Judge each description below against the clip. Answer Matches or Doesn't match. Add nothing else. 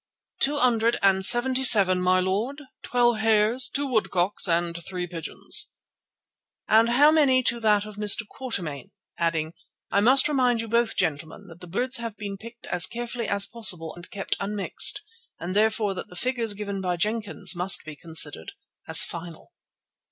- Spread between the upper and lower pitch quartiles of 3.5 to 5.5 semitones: Matches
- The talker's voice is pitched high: Matches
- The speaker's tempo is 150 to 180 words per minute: Matches